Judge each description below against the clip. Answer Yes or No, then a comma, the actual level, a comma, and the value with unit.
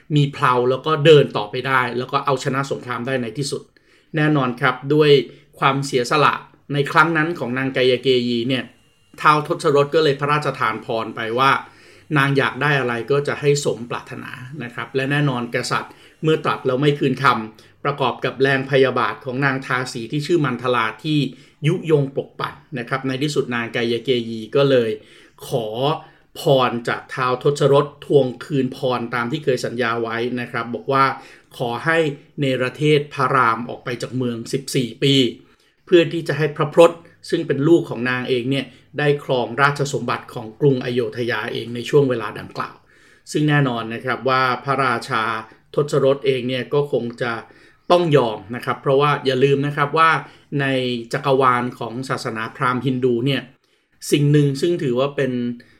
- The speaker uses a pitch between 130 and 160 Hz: Yes, low, 135 Hz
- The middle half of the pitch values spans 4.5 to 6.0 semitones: No, narrow, 2.6 semitones